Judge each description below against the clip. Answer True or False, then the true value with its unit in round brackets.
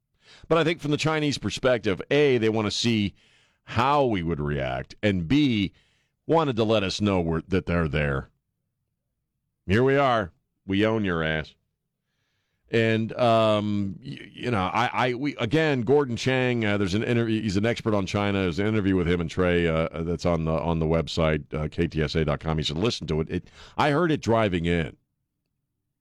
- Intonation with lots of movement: True (6.1 semitones)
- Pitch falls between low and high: False (105 Hz)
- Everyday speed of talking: True (185 wpm)